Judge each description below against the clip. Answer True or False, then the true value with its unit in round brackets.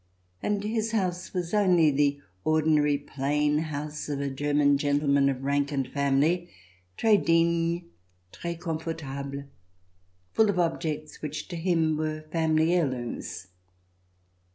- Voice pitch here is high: False (155 Hz)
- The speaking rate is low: True (130 wpm)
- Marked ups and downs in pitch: False (3.1 semitones)